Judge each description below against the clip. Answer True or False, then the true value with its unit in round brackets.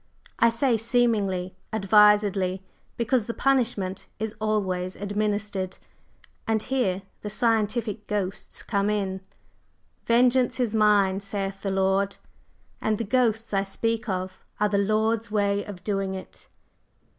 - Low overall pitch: False (210 Hz)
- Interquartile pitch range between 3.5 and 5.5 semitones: False (2.5 semitones)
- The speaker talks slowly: True (125 wpm)